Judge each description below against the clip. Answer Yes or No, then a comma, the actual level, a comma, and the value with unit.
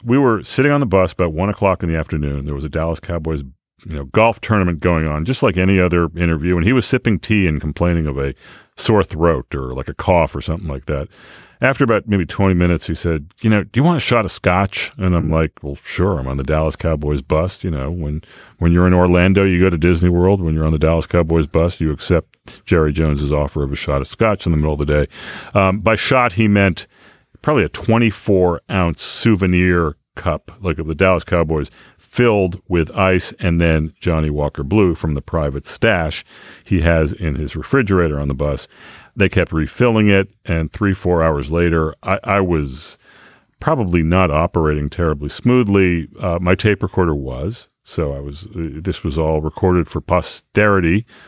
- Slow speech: No, fast, 205 wpm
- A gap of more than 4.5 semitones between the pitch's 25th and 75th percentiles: No, average, 3.8 semitones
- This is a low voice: Yes, very low, 85 Hz